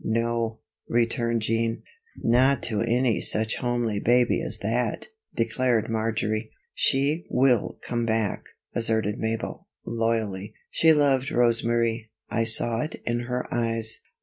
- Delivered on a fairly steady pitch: Yes, narrow, 1.4 semitones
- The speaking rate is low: Yes, slow, 125 wpm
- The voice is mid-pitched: No, low, 115 Hz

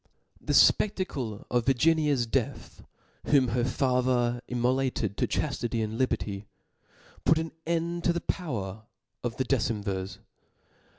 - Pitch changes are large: No, average, 4.7 semitones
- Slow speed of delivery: Yes, slow, 120 wpm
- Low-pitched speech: Yes, low, 125 Hz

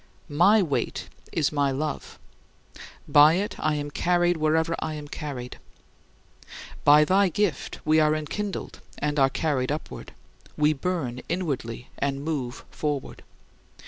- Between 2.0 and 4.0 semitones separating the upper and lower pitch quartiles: Yes, average, 2.8 semitones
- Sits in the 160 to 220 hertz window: No, medium, 150 Hz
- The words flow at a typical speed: No, slow, 130 wpm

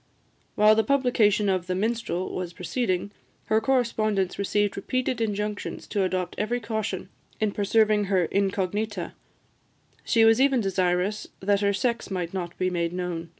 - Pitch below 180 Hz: No, high, 205 Hz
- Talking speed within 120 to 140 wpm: No, average, 150 wpm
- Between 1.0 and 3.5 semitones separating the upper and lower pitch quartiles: Yes, average, 3.1 semitones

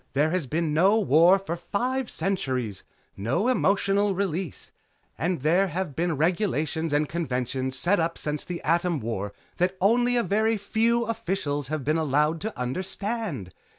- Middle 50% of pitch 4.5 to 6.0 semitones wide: Yes, average, 5.1 semitones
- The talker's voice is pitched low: No, medium, 170 Hz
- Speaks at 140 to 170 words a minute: Yes, average, 150 wpm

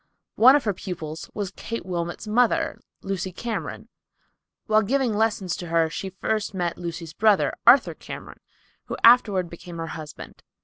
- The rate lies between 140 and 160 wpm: Yes, average, 150 wpm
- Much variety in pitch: No, average, 4.4 semitones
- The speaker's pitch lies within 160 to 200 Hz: Yes, high, 190 Hz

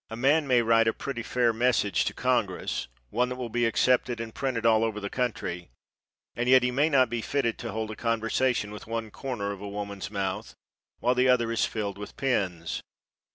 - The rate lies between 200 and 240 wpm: Yes, fast, 205 wpm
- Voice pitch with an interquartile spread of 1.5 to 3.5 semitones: Yes, average, 2.9 semitones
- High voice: No, low, 115 Hz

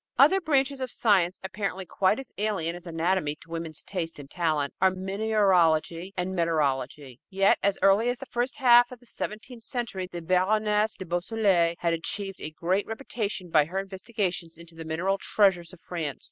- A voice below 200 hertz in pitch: Yes, high, 190 Hz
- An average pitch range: Yes, average, 4.3 semitones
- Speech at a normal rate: Yes, average, 175 wpm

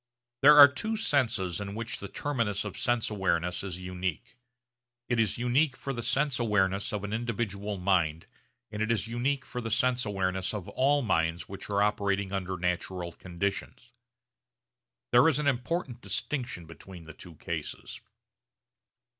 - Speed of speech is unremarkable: Yes, average, 155 wpm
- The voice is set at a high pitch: No, low, 105 Hz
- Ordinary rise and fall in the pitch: Yes, average, 4.8 semitones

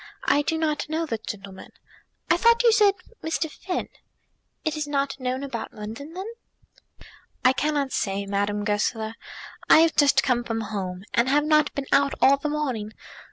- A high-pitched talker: Yes, very high, 275 Hz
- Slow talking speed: No, average, 170 wpm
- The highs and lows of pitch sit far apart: Yes, wide, 5.8 semitones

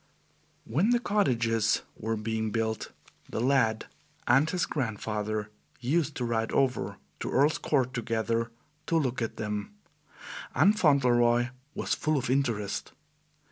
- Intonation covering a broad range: No, average, 4.0 semitones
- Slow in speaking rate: Yes, slow, 130 wpm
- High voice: No, low, 120 Hz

